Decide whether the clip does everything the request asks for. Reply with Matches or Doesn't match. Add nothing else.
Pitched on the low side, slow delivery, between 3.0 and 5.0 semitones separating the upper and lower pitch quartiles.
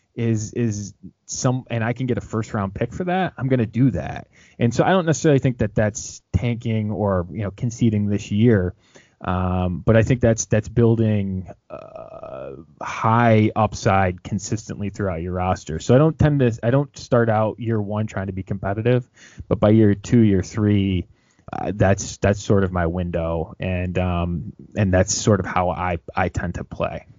Doesn't match